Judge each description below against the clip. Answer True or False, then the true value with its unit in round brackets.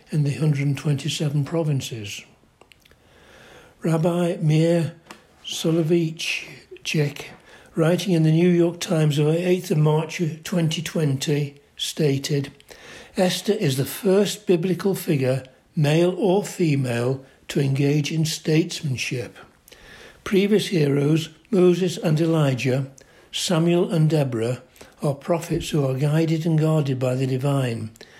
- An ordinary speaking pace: False (110 wpm)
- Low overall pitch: False (160 Hz)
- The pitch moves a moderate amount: True (3.4 semitones)